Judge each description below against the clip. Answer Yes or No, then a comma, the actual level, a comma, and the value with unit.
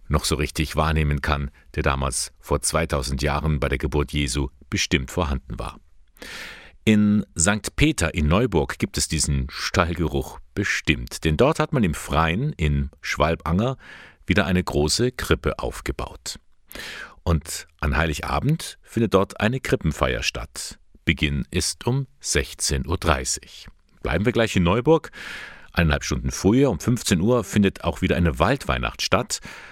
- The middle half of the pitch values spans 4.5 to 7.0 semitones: Yes, average, 4.8 semitones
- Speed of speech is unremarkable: Yes, average, 140 wpm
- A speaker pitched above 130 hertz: No, very low, 80 Hz